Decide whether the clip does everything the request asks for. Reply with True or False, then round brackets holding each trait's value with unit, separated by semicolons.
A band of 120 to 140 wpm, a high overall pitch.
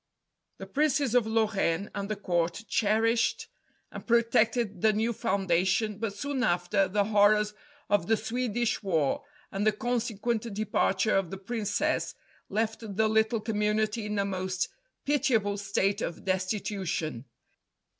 True (135 wpm; 210 Hz)